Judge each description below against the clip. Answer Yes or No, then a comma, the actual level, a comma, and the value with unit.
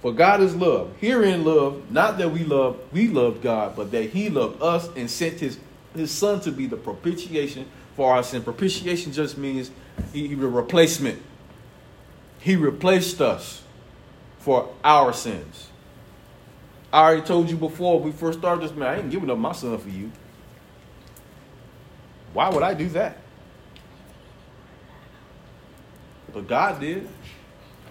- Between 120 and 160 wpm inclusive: Yes, average, 145 wpm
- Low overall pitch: No, medium, 155 Hz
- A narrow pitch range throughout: No, average, 4.8 semitones